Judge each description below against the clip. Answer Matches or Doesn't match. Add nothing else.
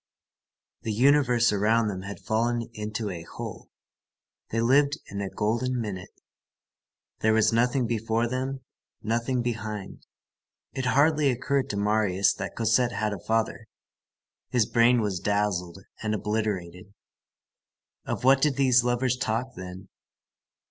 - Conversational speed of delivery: Doesn't match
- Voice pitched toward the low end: Matches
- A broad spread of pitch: Doesn't match